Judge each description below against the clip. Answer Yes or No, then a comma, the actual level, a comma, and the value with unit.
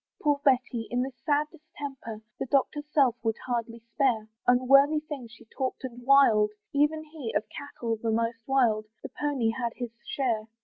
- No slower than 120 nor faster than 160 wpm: No, average, 170 wpm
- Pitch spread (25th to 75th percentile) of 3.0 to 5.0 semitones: Yes, average, 3.7 semitones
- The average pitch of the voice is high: Yes, very high, 250 Hz